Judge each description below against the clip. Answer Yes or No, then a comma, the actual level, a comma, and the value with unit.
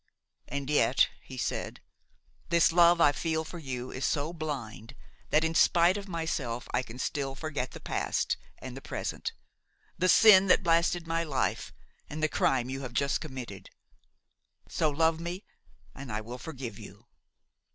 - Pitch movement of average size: Yes, average, 4.4 semitones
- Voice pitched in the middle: Yes, medium, 150 Hz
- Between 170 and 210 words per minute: No, average, 160 wpm